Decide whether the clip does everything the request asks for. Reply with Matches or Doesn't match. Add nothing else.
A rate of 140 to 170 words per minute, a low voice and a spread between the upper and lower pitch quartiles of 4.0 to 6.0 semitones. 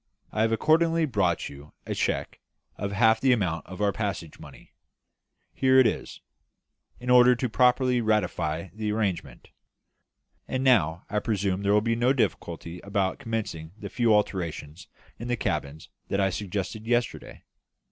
Matches